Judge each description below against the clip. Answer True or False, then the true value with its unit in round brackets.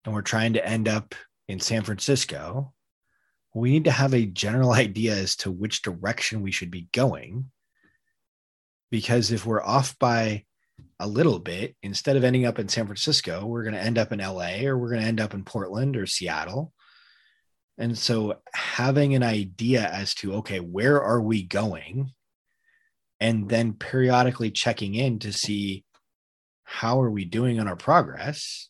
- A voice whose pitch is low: True (115 Hz)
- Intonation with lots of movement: False (3.8 semitones)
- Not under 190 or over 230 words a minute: False (170 wpm)